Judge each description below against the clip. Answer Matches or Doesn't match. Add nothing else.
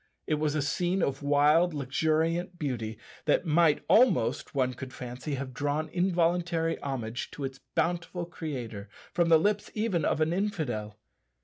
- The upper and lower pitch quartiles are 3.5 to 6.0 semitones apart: Matches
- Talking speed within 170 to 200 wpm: Doesn't match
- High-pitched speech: Doesn't match